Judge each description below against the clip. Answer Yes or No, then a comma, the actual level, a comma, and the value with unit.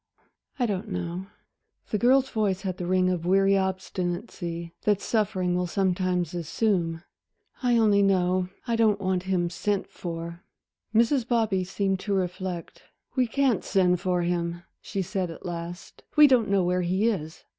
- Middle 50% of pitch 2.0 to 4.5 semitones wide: Yes, average, 2.8 semitones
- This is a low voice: No, medium, 185 Hz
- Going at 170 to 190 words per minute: No, average, 155 wpm